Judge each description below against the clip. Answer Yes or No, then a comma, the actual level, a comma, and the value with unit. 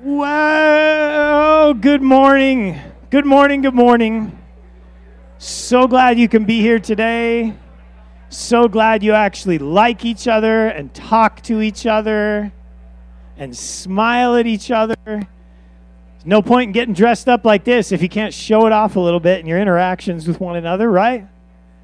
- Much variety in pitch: Yes, wide, 5.7 semitones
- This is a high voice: Yes, high, 220 Hz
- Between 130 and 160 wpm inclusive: Yes, average, 150 wpm